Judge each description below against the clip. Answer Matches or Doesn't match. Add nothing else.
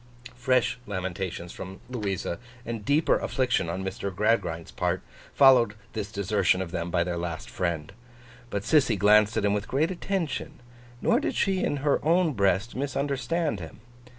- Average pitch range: Doesn't match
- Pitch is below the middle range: Matches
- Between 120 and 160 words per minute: Matches